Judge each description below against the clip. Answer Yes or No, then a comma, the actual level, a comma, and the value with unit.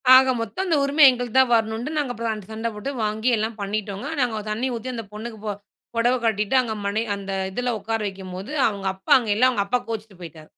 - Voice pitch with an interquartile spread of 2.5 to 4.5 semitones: Yes, average, 3.3 semitones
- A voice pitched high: Yes, high, 220 Hz